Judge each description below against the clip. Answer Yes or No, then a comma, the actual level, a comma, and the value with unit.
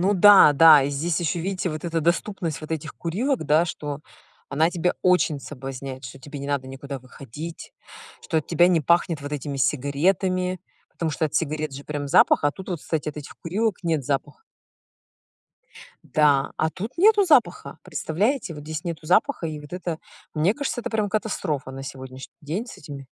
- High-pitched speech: No, medium, 160 Hz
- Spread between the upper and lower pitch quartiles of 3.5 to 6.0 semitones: Yes, average, 4.1 semitones